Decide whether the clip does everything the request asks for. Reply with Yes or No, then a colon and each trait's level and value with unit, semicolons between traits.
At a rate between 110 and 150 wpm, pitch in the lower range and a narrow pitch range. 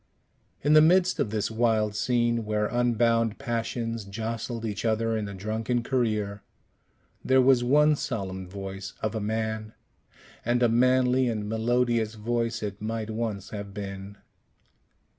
Yes: average, 140 wpm; low, 115 Hz; narrow, 2.2 semitones